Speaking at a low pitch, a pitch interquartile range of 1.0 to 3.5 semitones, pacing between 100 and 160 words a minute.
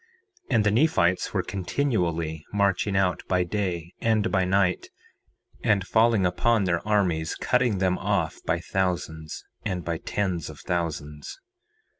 Yes: very low, 95 Hz; average, 3.2 semitones; average, 145 wpm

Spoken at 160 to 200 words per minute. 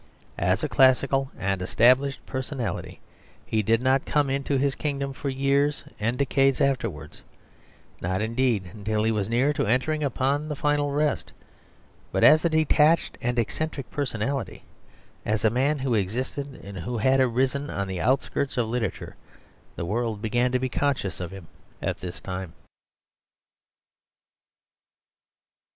No: average, 145 wpm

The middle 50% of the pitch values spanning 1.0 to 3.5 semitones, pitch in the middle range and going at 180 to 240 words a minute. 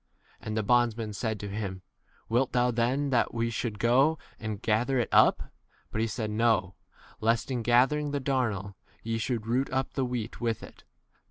No: narrow, 2.6 semitones; low, 115 Hz; average, 200 wpm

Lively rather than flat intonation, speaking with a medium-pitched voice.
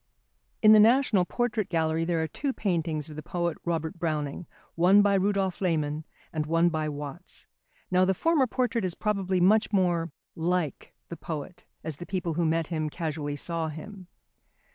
No: average, 3.6 semitones; medium, 170 Hz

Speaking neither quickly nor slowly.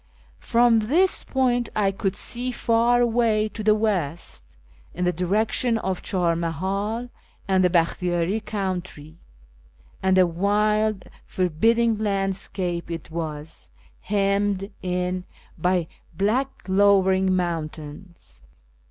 No: slow, 115 wpm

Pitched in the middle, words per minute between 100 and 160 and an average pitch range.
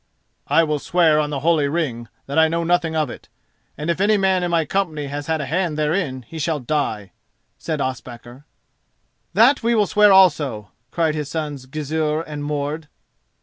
No: medium, 155 Hz; average, 185 wpm; average, 3.0 semitones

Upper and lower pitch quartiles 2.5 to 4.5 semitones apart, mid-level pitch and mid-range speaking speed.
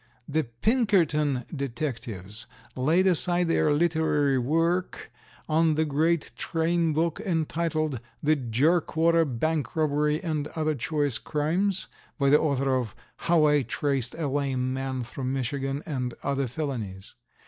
No: average, 3.5 semitones; medium, 150 Hz; slow, 125 wpm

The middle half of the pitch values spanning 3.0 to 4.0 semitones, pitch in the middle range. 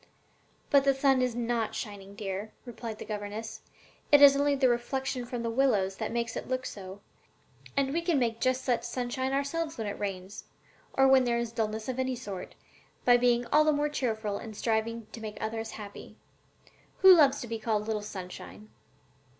No: average, 3.6 semitones; high, 235 Hz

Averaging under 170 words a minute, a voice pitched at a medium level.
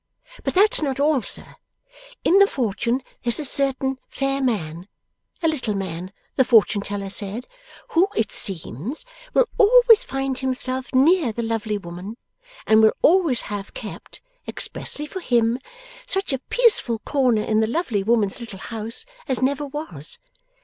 No: average, 150 wpm; very high, 250 Hz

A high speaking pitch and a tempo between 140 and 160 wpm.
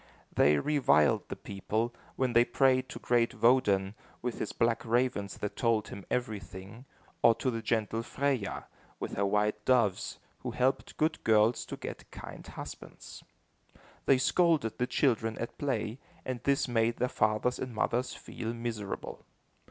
No: low, 115 Hz; average, 150 wpm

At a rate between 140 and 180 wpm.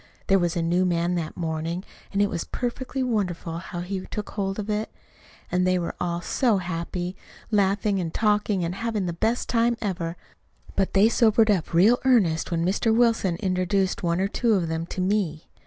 No: average, 190 wpm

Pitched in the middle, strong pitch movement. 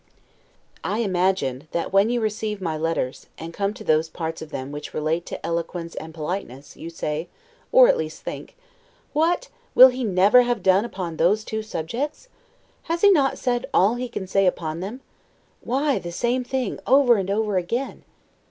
No: high, 195 Hz; wide, 6.8 semitones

